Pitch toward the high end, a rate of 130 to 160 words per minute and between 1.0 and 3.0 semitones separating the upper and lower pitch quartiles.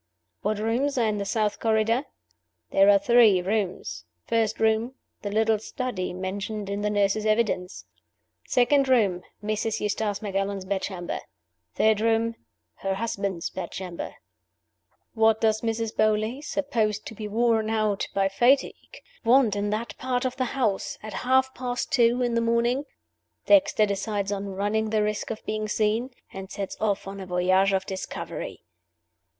Yes: high, 215 Hz; average, 150 wpm; narrow, 2.6 semitones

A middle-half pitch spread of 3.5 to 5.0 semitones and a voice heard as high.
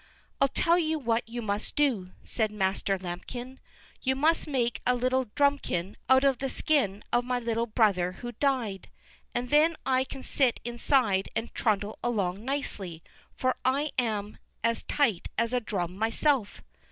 Yes: average, 4.4 semitones; high, 240 Hz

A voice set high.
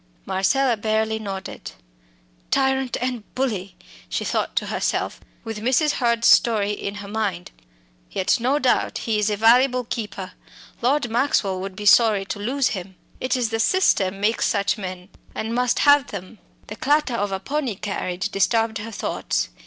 Yes: high, 220 Hz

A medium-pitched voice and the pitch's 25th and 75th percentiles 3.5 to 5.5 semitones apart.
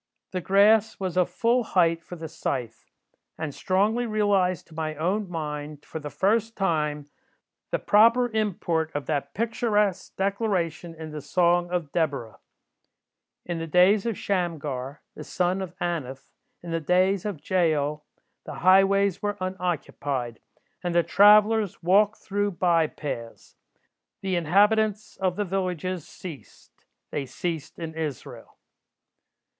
Yes: medium, 180 Hz; average, 4.1 semitones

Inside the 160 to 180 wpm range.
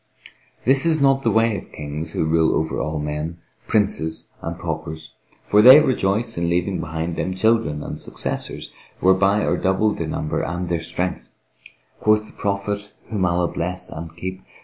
Yes: average, 170 wpm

